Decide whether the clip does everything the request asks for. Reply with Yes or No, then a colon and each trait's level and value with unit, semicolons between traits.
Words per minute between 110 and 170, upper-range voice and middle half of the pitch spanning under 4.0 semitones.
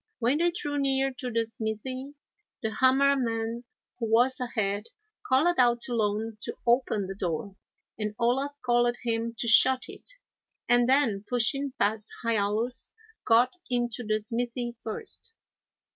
Yes: average, 145 wpm; high, 240 Hz; average, 2.8 semitones